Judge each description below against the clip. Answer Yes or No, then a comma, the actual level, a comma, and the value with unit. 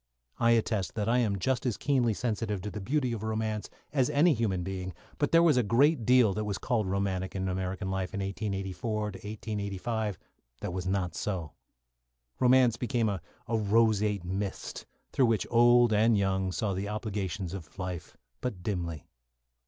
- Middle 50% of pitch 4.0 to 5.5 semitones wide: No, average, 3.4 semitones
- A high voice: No, low, 105 Hz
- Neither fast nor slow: Yes, average, 170 wpm